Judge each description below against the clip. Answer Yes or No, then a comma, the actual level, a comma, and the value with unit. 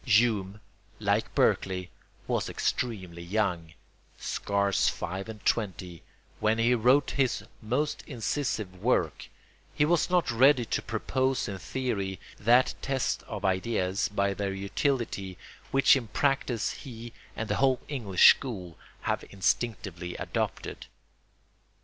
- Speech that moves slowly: Yes, slow, 120 wpm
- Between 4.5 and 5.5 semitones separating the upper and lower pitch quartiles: Yes, average, 4.9 semitones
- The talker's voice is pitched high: No, low, 110 Hz